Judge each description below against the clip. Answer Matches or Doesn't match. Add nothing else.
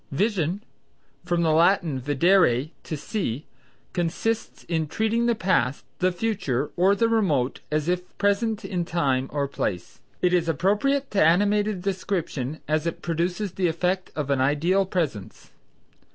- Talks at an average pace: Matches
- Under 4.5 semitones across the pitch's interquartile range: Doesn't match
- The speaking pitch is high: Doesn't match